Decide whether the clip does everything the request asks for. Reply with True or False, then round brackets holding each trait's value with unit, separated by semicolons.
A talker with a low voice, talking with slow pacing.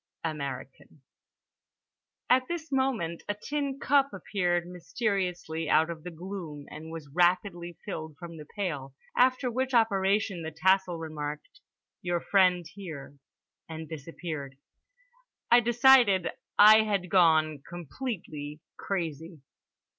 False (175 Hz; 115 wpm)